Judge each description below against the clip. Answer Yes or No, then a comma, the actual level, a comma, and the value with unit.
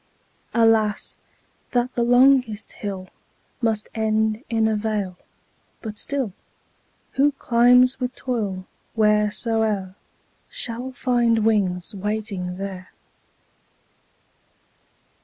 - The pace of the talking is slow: Yes, slow, 90 wpm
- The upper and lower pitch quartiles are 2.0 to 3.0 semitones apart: Yes, average, 2.7 semitones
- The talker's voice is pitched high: Yes, high, 220 Hz